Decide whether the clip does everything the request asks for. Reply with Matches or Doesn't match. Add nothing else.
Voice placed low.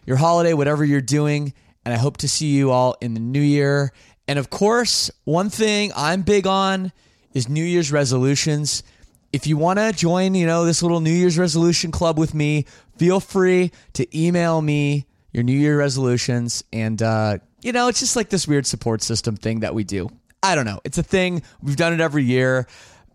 Doesn't match